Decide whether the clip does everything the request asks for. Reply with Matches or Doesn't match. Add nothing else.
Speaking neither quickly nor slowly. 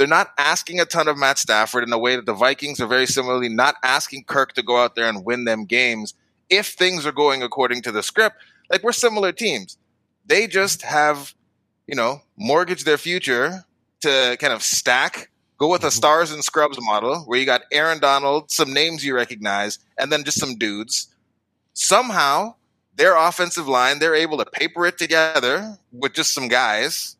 Matches